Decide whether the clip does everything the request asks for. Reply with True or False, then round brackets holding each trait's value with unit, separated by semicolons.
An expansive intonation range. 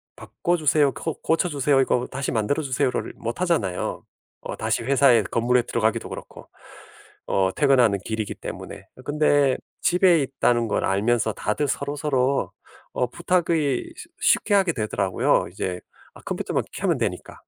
False (4.6 semitones)